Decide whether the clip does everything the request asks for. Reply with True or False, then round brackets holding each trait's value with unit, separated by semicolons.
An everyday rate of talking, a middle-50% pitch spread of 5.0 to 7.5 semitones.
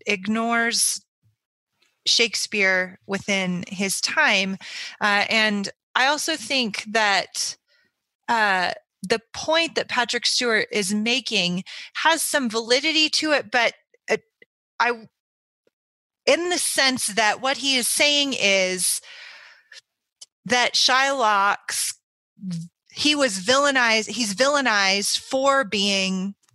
False (100 wpm; 5.6 semitones)